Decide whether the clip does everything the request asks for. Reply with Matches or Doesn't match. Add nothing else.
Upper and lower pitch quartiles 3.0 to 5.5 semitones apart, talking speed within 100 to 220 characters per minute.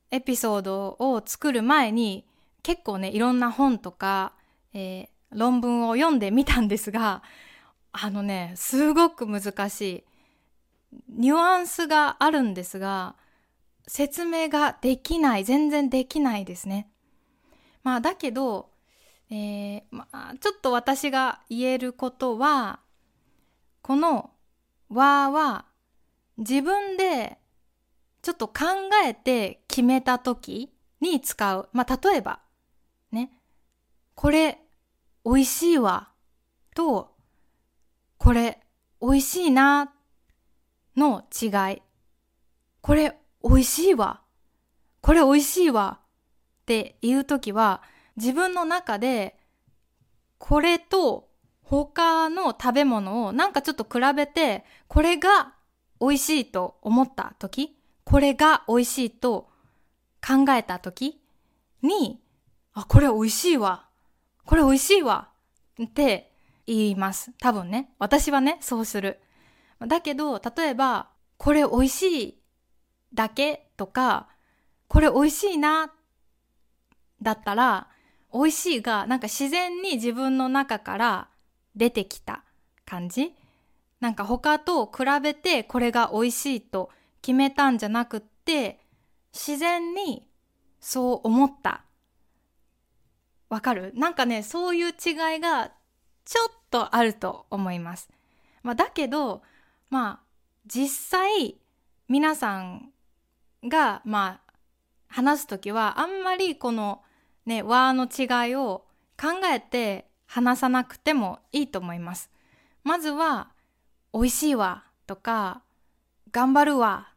Matches